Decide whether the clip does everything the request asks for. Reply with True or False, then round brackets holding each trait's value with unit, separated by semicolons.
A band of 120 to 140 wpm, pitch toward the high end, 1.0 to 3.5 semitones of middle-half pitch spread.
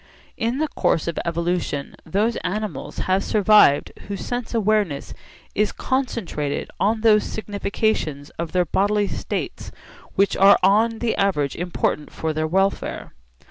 False (135 wpm; 200 Hz; 4.3 semitones)